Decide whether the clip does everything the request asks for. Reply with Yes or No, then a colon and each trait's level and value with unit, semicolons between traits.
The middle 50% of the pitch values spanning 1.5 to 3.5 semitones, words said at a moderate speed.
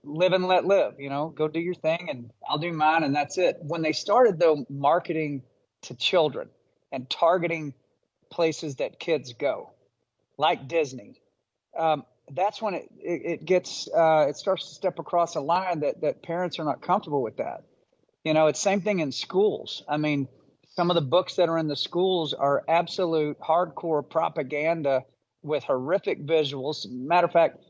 Yes: average, 3.2 semitones; average, 180 wpm